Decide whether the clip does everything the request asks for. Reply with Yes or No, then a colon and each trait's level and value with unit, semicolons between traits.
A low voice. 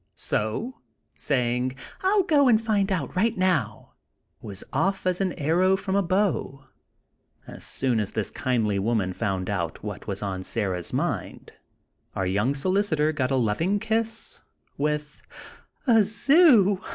No: medium, 150 Hz